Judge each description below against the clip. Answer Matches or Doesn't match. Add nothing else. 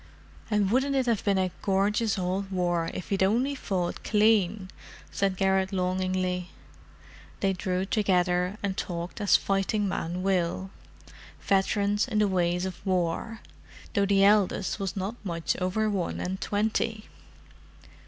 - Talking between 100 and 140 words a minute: Matches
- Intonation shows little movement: Matches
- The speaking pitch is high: Matches